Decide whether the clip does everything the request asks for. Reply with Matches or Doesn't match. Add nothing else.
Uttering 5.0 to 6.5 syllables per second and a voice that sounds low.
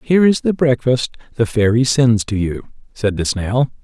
Doesn't match